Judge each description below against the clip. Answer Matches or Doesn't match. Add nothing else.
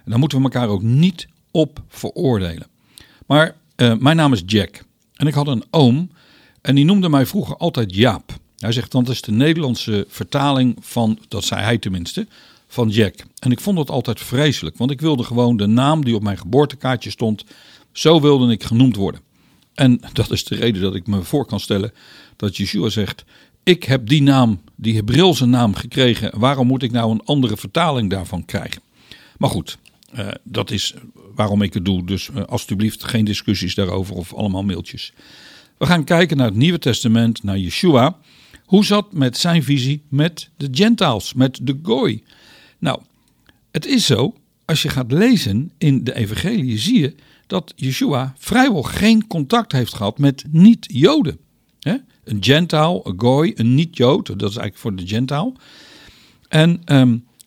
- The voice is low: Matches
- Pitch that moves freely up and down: Matches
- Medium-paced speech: Matches